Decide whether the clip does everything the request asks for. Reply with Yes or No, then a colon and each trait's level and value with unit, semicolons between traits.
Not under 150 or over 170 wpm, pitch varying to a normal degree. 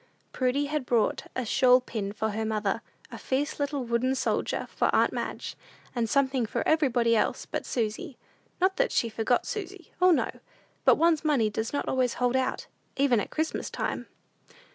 No: average, 180 wpm; average, 4.0 semitones